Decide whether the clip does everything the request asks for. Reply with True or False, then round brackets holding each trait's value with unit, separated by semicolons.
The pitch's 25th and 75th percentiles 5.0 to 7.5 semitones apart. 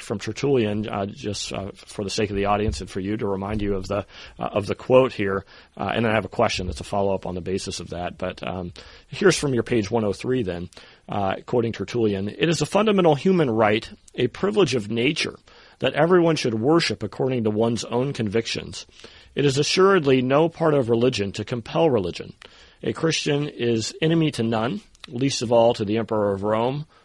True (5.4 semitones)